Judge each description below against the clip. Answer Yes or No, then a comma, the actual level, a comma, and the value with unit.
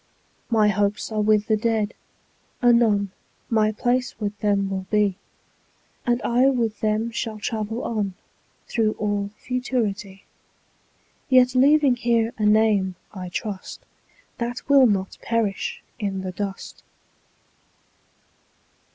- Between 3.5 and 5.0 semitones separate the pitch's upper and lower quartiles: No, narrow, 2.6 semitones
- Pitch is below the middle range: No, high, 215 Hz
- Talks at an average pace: No, slow, 120 wpm